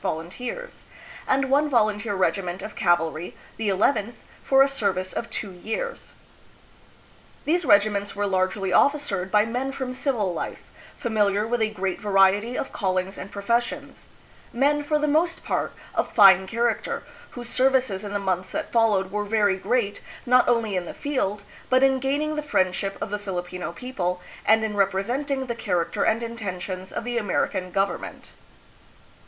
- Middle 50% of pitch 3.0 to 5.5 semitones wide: Yes, average, 4.8 semitones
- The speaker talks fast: No, average, 160 wpm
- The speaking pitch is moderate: No, high, 210 Hz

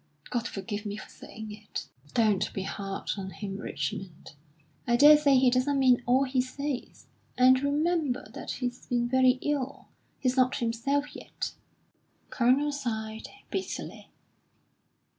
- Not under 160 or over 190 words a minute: No, average, 140 wpm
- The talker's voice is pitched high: Yes, very high, 250 Hz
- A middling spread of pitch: Yes, average, 4.0 semitones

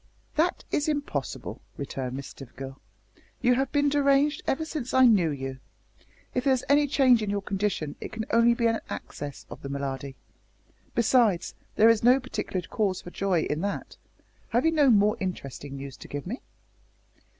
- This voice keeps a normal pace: Yes, average, 175 wpm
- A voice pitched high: Yes, high, 215 Hz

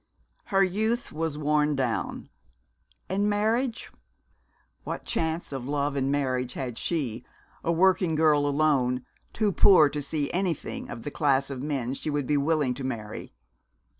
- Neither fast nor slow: Yes, average, 150 wpm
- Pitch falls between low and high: Yes, medium, 145 Hz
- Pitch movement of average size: Yes, average, 3.9 semitones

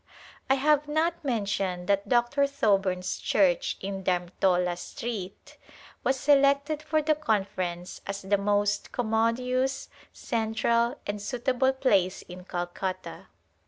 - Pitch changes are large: Yes, wide, 5.9 semitones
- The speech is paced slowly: Yes, slow, 115 wpm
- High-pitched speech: Yes, high, 220 Hz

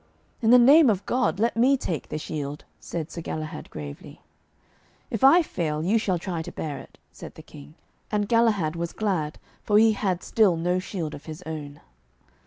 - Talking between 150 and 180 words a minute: No, average, 190 wpm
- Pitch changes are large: Yes, wide, 6.1 semitones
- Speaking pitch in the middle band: Yes, medium, 180 Hz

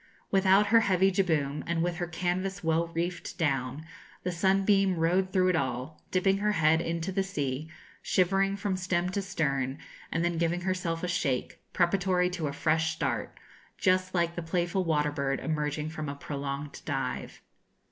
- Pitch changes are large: No, average, 3.2 semitones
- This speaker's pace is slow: No, average, 165 wpm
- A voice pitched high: No, medium, 175 Hz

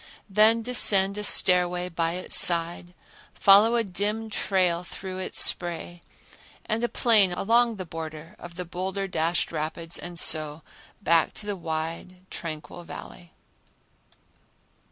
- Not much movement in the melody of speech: No, average, 3.2 semitones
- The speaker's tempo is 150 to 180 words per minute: No, slow, 135 wpm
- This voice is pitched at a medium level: Yes, medium, 180 Hz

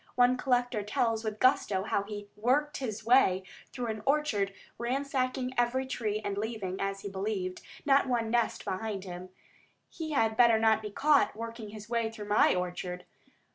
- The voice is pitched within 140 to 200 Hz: No, high, 220 Hz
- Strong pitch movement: No, average, 3.6 semitones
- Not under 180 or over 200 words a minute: No, average, 170 wpm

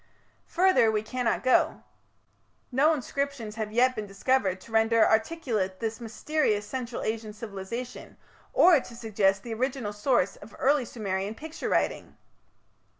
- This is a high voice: Yes, high, 230 Hz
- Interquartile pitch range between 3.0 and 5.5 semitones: Yes, average, 3.6 semitones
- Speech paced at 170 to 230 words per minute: No, slow, 135 wpm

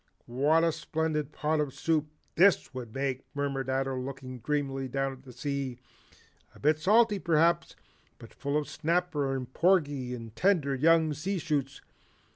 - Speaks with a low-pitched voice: No, medium, 145 Hz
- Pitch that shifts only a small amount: No, average, 3.3 semitones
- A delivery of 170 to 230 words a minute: No, average, 155 wpm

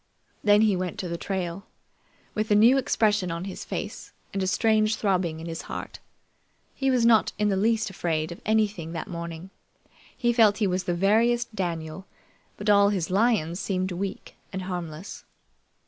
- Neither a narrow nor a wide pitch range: Yes, average, 3.6 semitones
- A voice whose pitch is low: No, high, 195 Hz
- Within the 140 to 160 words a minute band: No, average, 175 wpm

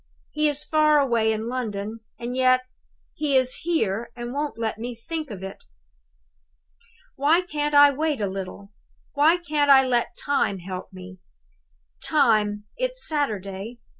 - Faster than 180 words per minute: No, average, 145 wpm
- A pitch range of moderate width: No, wide, 5.7 semitones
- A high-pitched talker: Yes, very high, 255 Hz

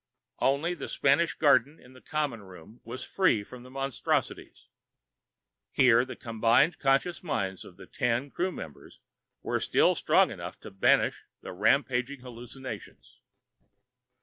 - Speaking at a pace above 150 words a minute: No, slow, 135 wpm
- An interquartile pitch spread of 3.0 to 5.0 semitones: Yes, average, 3.5 semitones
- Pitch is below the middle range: Yes, low, 130 Hz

